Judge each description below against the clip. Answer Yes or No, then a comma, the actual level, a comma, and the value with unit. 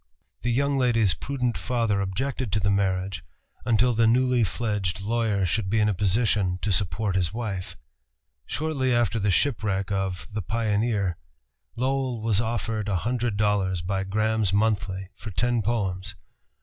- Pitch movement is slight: No, average, 3.5 semitones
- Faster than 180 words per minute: No, average, 150 wpm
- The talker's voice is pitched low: Yes, low, 105 Hz